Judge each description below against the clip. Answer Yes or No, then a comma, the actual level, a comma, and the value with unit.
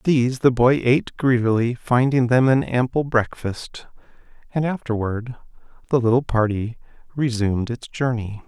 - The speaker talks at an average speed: No, slow, 125 wpm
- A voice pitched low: Yes, low, 120 Hz